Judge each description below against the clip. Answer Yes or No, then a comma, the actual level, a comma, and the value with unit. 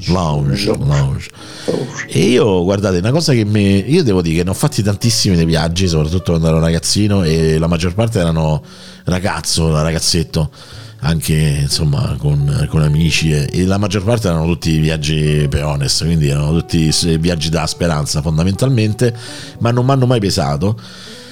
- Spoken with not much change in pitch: No, wide, 5.5 semitones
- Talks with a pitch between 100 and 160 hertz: No, very low, 90 Hz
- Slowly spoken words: No, average, 160 wpm